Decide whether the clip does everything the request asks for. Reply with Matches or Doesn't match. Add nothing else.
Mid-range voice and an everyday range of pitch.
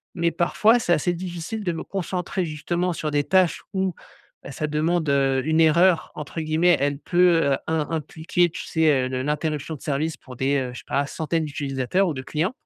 Matches